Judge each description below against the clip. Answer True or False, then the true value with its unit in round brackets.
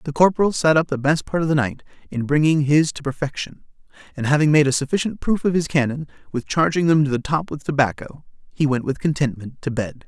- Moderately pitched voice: True (145 Hz)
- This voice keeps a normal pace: False (220 wpm)